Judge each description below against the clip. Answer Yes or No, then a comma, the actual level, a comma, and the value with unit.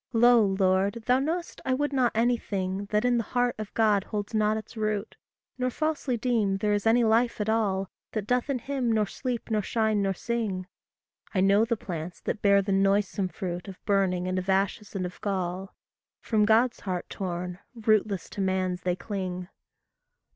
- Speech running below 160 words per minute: No, average, 185 wpm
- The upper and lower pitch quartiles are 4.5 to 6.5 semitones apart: No, average, 3.4 semitones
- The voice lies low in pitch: No, high, 210 Hz